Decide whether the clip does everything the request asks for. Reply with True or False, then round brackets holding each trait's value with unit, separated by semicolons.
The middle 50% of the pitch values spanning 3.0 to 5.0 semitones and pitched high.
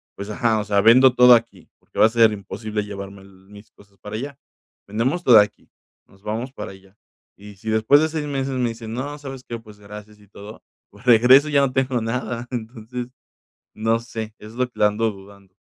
False (3.3 semitones; 110 Hz)